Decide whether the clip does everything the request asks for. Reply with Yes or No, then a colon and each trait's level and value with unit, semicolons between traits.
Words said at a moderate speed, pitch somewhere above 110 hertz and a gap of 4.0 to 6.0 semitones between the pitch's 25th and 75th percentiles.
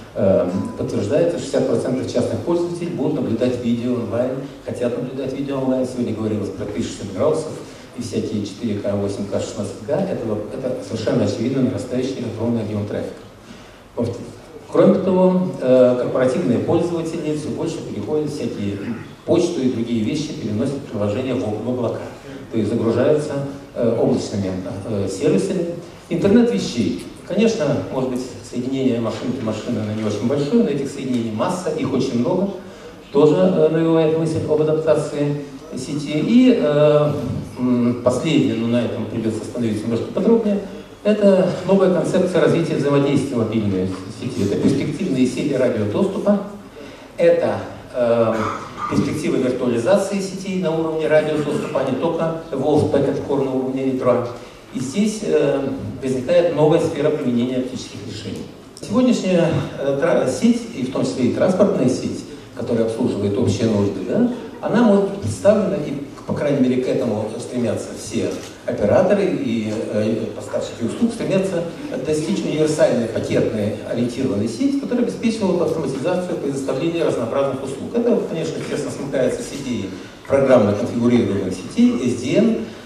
Yes: average, 130 wpm; low, 135 Hz; wide, 5.6 semitones